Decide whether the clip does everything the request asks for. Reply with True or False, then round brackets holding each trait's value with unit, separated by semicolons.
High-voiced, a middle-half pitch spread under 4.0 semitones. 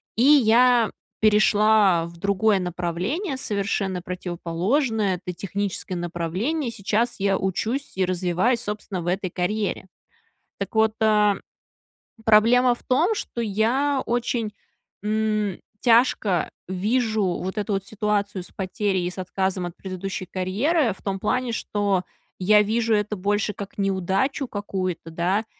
True (205 Hz; 3.3 semitones)